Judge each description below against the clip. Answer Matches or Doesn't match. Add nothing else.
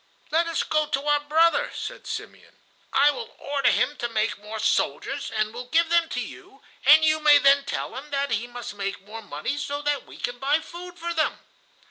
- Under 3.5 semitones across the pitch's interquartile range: Doesn't match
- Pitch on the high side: Matches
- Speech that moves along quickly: Matches